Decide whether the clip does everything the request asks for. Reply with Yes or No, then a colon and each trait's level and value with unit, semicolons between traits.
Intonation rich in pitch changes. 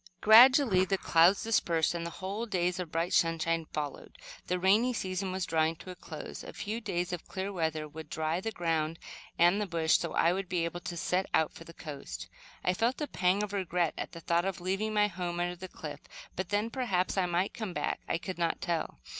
No: average, 2.8 semitones